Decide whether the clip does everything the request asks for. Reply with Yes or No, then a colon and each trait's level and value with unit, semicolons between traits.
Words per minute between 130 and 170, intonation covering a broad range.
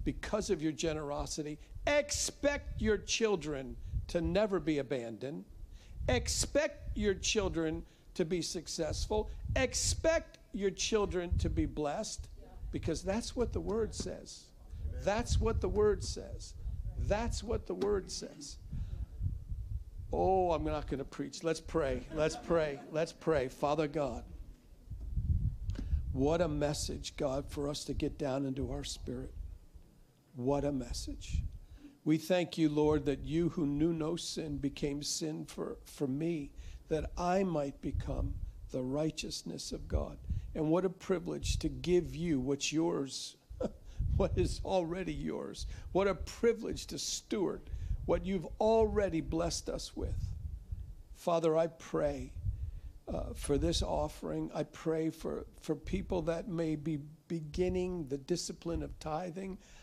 Yes: average, 140 wpm; wide, 5.9 semitones